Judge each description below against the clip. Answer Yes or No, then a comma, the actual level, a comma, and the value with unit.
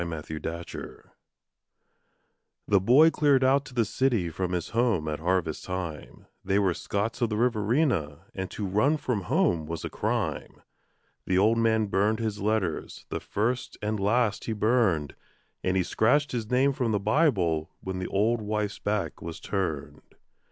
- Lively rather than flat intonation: No, average, 4.5 semitones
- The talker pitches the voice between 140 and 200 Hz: No, low, 105 Hz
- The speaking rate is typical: Yes, average, 165 wpm